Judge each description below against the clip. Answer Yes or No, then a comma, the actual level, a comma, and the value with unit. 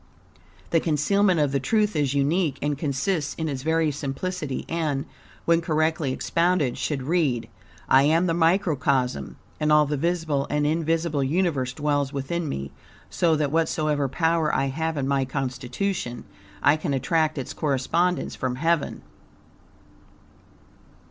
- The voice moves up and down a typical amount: Yes, average, 3.3 semitones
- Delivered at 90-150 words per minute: Yes, average, 140 wpm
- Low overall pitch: No, medium, 150 Hz